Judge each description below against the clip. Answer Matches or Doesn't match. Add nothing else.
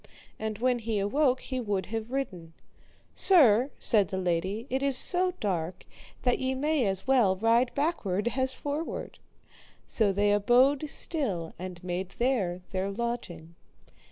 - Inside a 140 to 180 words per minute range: Matches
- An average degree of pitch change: Doesn't match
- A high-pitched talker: Matches